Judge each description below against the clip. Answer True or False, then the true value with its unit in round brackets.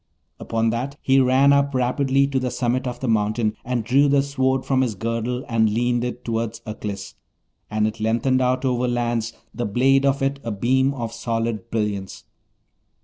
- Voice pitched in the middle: False (120 Hz)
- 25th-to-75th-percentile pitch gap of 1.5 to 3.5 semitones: True (2.6 semitones)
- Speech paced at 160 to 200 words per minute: True (180 wpm)